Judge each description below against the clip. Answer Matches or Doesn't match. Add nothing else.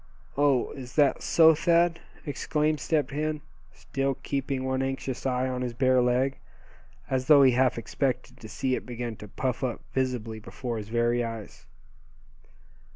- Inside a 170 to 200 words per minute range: Doesn't match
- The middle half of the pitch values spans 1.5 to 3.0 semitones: Matches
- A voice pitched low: Matches